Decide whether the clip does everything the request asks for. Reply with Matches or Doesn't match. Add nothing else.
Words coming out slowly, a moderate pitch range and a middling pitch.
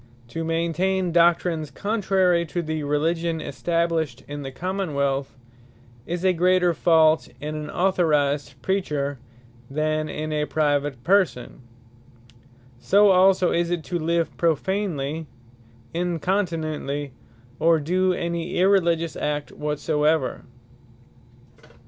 Matches